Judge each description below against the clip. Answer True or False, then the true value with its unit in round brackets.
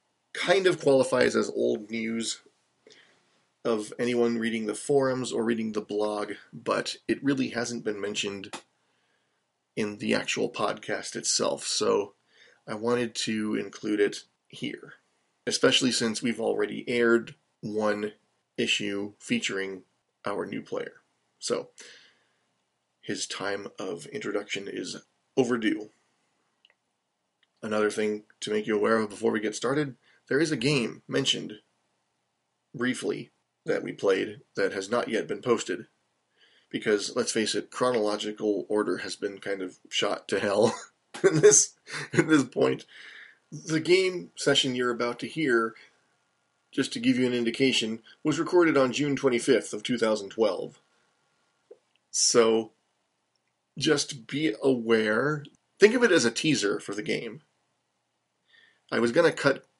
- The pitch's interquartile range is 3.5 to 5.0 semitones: True (4.3 semitones)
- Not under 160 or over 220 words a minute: False (135 wpm)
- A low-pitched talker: True (115 Hz)